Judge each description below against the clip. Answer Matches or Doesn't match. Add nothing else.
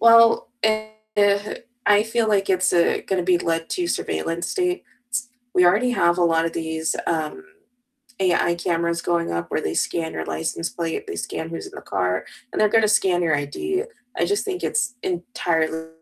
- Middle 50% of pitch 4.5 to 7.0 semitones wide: Matches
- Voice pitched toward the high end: Doesn't match